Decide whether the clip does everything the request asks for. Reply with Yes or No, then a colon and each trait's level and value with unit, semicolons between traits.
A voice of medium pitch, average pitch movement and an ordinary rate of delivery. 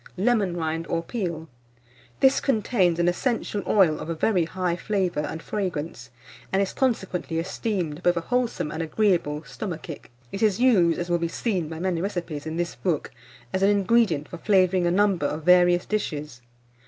Yes: medium, 175 Hz; average, 3.6 semitones; average, 175 wpm